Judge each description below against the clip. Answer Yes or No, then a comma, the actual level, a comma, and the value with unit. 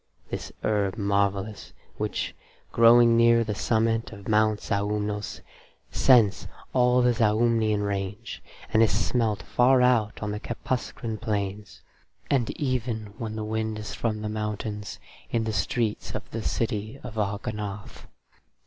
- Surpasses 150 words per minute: No, slow, 135 wpm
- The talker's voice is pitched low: Yes, low, 110 Hz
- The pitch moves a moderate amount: No, narrow, 2.0 semitones